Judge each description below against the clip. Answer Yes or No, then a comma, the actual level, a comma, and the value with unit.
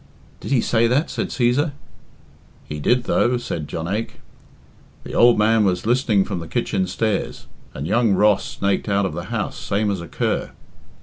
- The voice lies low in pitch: Yes, low, 105 Hz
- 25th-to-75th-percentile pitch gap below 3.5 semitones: No, average, 4.0 semitones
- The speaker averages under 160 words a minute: No, average, 175 wpm